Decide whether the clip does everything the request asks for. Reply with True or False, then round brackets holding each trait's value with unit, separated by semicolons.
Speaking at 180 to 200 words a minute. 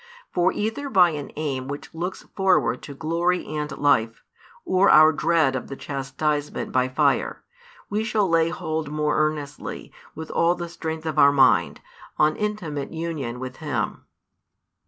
False (155 wpm)